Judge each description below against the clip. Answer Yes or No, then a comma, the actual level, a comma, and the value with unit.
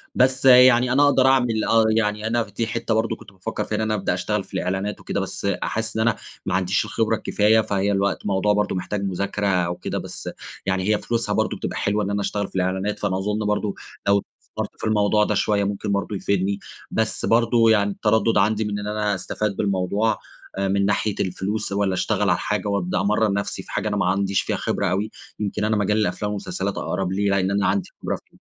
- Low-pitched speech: Yes, low, 105 Hz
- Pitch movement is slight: Yes, narrow, 1.8 semitones